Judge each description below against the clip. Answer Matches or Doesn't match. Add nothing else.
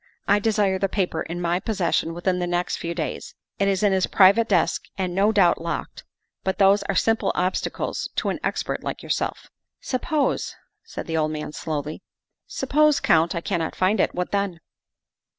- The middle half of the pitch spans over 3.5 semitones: Doesn't match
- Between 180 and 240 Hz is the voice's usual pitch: Matches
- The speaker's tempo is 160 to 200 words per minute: Matches